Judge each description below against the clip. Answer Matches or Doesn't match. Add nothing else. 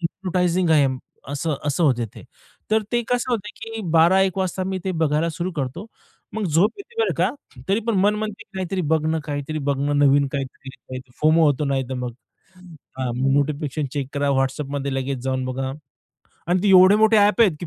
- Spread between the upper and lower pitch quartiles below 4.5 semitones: Doesn't match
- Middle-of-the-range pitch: Matches